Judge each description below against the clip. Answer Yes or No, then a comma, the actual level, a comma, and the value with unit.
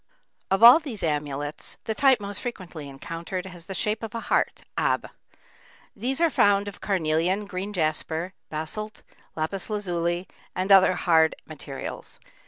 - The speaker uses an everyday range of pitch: Yes, average, 4.6 semitones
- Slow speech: No, average, 145 wpm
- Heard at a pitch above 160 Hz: Yes, medium, 185 Hz